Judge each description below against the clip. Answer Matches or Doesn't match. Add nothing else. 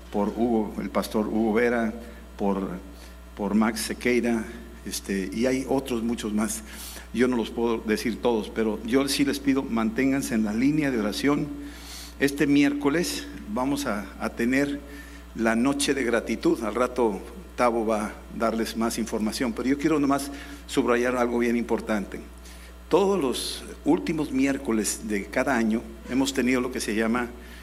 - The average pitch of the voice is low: Matches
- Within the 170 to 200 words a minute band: Doesn't match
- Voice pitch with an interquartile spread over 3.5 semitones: Matches